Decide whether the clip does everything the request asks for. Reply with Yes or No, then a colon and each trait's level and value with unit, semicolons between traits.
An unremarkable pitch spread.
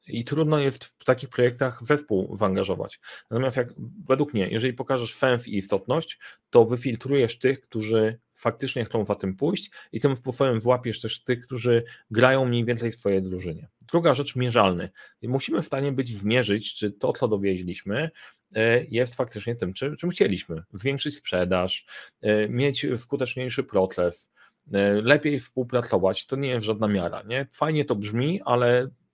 Yes: average, 3.8 semitones